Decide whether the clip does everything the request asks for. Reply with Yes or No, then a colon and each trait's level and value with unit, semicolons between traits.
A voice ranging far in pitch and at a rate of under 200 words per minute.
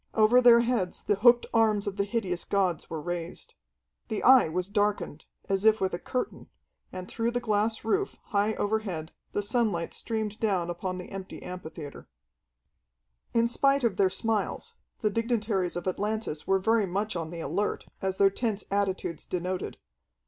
No: average, 3.5 semitones; average, 165 wpm